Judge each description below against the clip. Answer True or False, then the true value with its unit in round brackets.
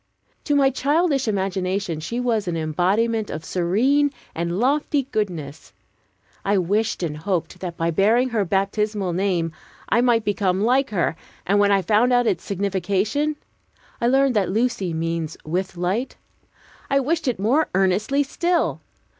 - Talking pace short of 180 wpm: True (150 wpm)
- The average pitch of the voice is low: False (205 Hz)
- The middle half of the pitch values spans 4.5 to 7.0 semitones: True (5.4 semitones)